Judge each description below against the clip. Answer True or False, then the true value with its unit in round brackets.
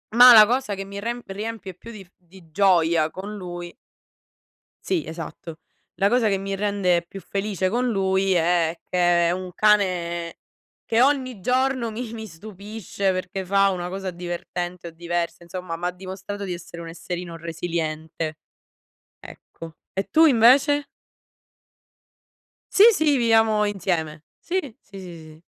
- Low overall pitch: False (190 Hz)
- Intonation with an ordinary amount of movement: True (3.8 semitones)